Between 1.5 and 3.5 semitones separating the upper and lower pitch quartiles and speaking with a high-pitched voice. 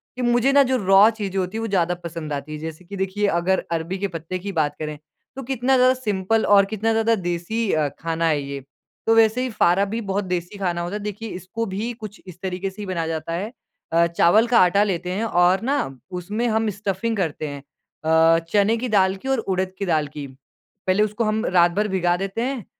No: average, 4.3 semitones; high, 195 Hz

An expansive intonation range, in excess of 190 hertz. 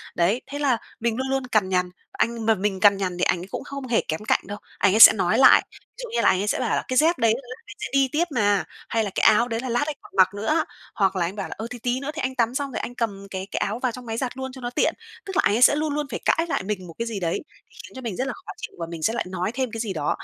No: average, 4.8 semitones; high, 230 Hz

